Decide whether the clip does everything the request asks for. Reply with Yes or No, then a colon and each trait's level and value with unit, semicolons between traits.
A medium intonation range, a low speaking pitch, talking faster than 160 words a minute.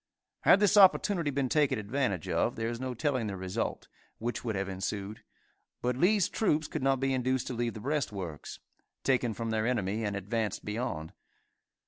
Yes: average, 4.6 semitones; low, 120 Hz; average, 175 wpm